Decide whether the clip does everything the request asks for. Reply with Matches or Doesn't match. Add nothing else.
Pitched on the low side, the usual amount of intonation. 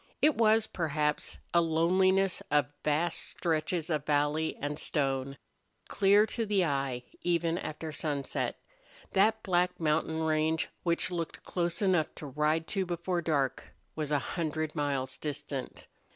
Doesn't match